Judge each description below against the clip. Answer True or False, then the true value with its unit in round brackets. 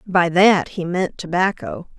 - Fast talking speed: False (150 wpm)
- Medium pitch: True (180 Hz)